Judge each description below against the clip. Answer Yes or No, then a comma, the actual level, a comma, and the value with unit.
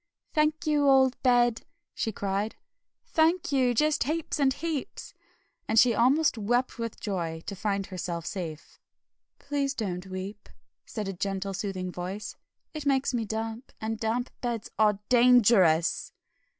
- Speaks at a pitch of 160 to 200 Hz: No, high, 225 Hz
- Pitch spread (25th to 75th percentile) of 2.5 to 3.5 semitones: No, average, 5.3 semitones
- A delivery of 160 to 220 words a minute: No, average, 140 wpm